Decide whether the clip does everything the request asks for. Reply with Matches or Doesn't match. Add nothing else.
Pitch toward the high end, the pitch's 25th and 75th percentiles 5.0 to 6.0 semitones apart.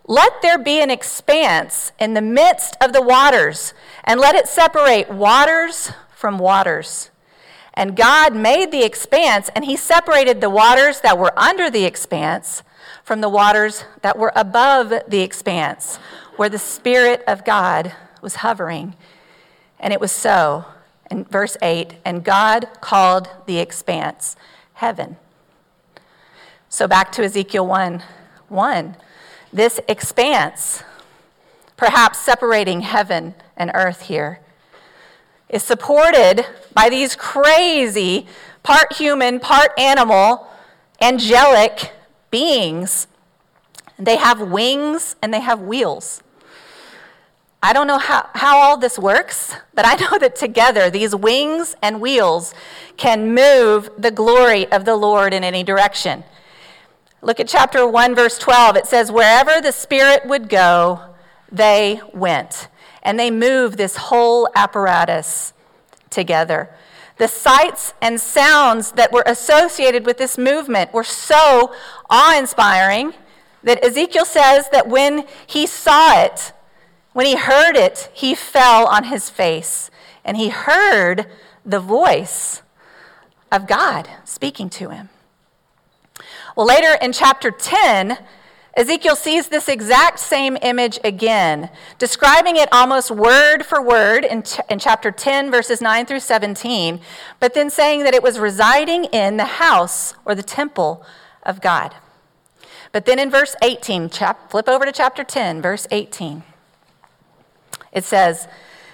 Matches